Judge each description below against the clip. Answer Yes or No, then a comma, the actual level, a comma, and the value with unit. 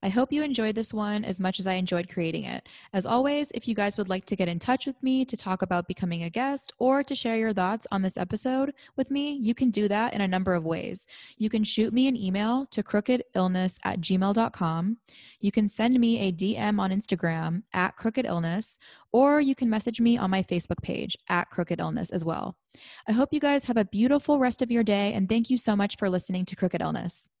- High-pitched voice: Yes, high, 210 Hz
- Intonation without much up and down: No, average, 4.9 semitones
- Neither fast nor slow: No, fast, 230 wpm